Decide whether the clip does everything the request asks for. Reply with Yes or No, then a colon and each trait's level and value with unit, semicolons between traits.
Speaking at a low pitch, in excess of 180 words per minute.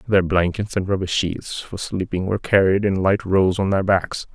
Yes: very low, 95 Hz; fast, 205 wpm